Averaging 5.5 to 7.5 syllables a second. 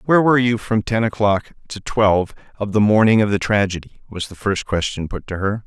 Yes: 5.8 syllables/s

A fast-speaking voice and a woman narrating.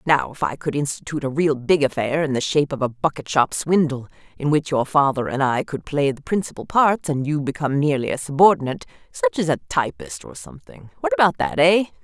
Yes: fast, 210 wpm; female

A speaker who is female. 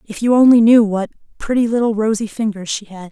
Yes: female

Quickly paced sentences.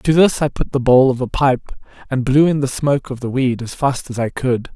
Yes: fast, 280 wpm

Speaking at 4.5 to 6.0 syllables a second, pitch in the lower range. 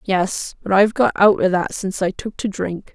No: 5.1 syllables/s; high, 195 Hz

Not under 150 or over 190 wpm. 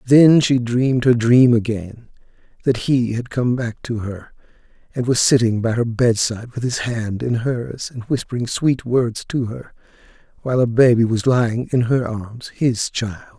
Yes: average, 175 wpm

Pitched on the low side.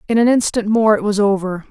No: high, 210 Hz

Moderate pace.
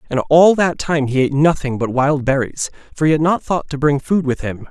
No: fast, 255 wpm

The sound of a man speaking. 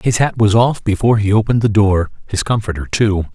Yes: male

